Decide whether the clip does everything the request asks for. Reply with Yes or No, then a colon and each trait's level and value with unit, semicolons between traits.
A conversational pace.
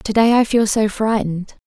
Yes: average, 180 wpm